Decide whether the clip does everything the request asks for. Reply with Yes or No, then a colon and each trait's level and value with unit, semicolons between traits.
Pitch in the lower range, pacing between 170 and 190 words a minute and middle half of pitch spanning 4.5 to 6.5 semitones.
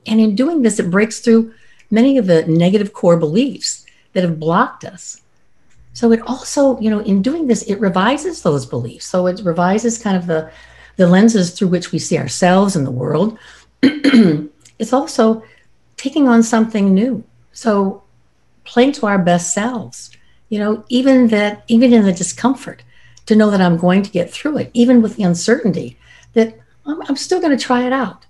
No: high, 215 Hz; average, 185 wpm; average, 5.3 semitones